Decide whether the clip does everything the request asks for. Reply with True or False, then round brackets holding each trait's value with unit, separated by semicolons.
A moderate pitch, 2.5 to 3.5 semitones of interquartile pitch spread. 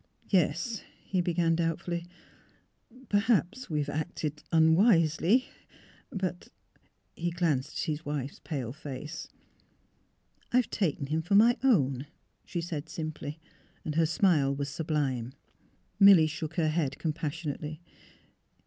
True (160 Hz; 3.0 semitones)